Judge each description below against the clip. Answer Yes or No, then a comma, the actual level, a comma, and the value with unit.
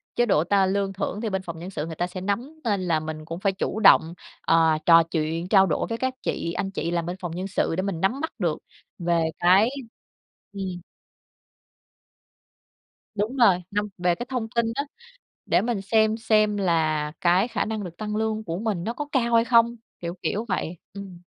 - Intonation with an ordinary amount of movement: Yes, average, 4.3 semitones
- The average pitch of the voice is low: No, high, 195 Hz